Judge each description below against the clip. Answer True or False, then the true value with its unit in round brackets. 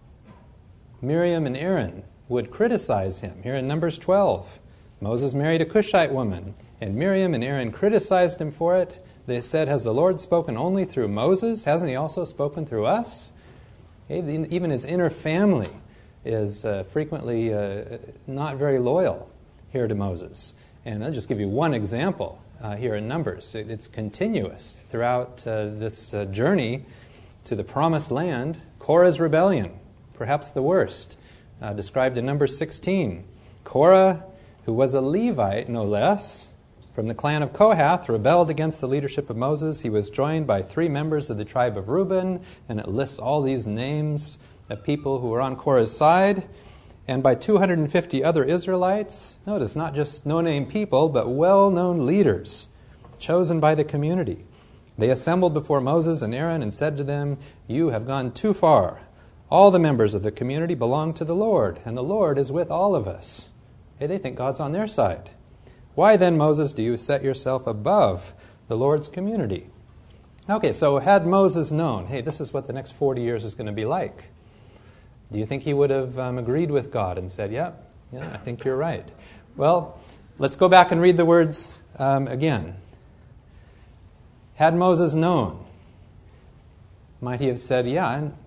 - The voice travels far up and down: True (6.6 semitones)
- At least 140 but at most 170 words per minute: True (165 wpm)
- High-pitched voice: False (135 Hz)